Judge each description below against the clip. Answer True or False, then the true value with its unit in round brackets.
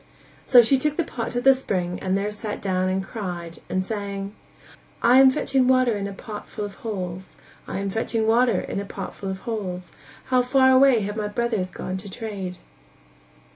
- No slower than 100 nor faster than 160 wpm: False (200 wpm)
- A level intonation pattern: False (4.2 semitones)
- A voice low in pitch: False (210 Hz)